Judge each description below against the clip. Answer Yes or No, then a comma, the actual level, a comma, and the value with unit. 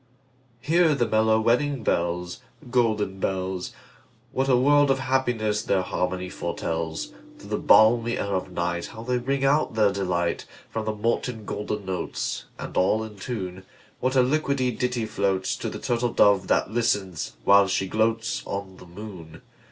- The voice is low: Yes, low, 110 Hz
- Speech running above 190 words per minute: No, slow, 135 wpm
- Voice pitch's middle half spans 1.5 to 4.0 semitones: No, average, 4.6 semitones